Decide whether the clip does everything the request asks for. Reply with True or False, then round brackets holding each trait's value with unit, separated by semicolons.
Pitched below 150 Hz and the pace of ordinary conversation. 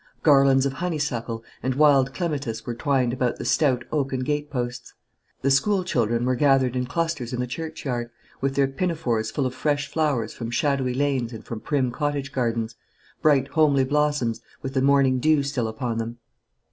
True (135 Hz; 175 wpm)